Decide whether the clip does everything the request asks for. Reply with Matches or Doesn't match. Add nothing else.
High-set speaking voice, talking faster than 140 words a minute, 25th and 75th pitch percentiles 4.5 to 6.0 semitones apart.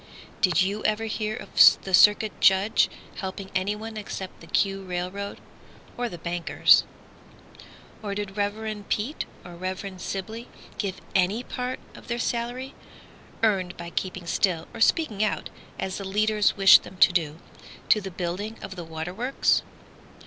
Doesn't match